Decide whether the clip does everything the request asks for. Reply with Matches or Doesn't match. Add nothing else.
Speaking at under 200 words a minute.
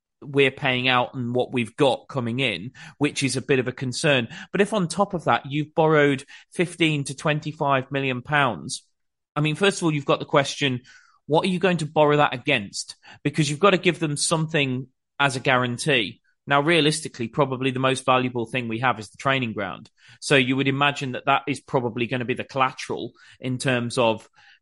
Doesn't match